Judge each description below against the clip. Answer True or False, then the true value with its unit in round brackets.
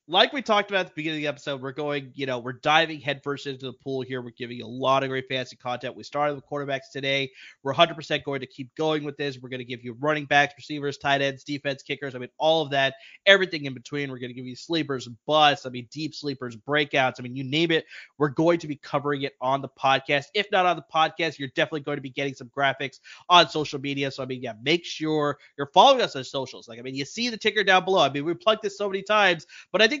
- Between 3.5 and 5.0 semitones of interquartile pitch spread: False (2.8 semitones)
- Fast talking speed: True (275 wpm)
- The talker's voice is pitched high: False (140 Hz)